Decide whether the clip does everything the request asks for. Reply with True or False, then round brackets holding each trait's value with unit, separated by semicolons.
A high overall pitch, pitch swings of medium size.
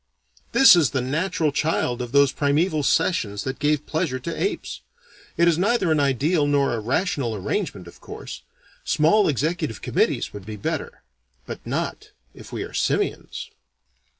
False (145 Hz; 4.9 semitones)